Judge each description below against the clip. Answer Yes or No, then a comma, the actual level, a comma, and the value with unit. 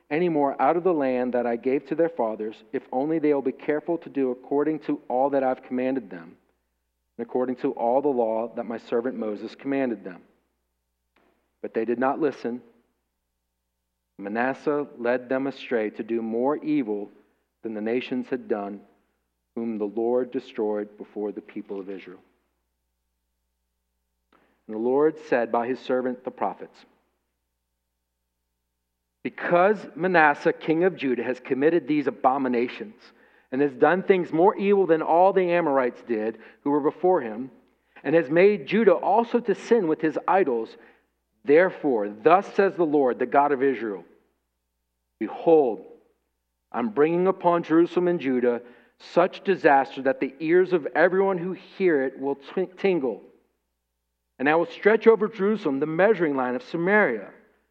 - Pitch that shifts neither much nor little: No, wide, 8.1 semitones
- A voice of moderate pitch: No, low, 130 Hz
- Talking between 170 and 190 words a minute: No, average, 155 wpm